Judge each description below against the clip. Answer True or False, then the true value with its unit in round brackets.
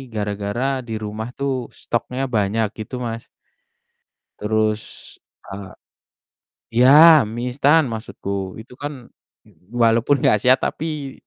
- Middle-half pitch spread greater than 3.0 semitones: True (4.1 semitones)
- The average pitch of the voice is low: True (115 Hz)